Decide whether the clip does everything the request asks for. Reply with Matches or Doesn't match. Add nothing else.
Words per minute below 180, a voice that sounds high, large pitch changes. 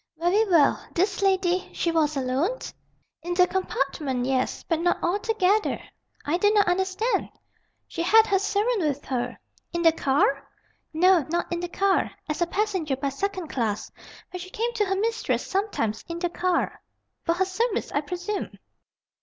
Doesn't match